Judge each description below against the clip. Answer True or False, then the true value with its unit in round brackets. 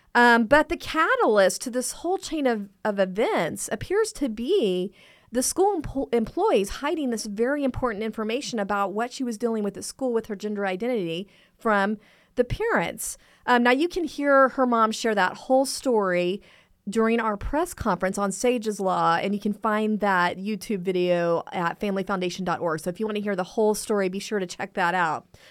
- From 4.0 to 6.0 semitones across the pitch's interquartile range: True (4.4 semitones)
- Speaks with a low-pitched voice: False (220 Hz)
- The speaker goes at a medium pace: True (190 wpm)